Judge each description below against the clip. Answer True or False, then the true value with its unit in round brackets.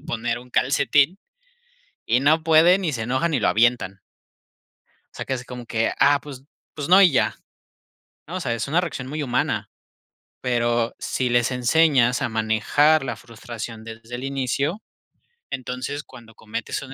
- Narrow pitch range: False (3.9 semitones)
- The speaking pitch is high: False (125 Hz)